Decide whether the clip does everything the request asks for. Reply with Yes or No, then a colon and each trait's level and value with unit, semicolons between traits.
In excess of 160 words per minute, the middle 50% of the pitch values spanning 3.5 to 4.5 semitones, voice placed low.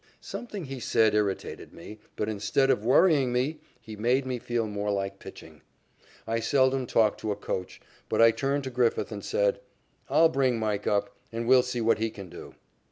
Yes: average, 190 wpm; average, 3.9 semitones; low, 115 Hz